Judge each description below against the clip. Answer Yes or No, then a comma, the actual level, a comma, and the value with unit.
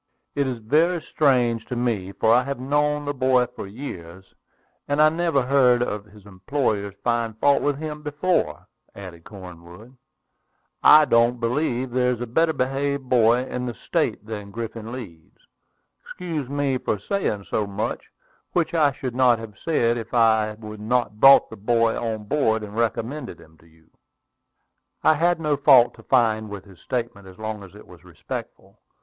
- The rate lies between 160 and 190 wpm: Yes, average, 175 wpm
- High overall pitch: No, low, 120 Hz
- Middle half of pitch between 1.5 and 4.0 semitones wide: No, average, 4.6 semitones